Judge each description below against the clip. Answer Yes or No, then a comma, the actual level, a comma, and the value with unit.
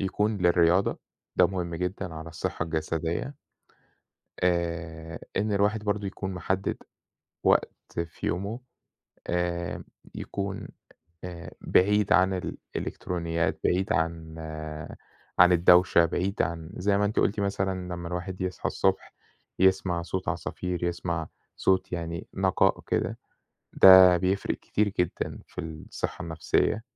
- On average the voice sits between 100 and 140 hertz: No, very low, 90 Hz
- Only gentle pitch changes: Yes, narrow, 2.3 semitones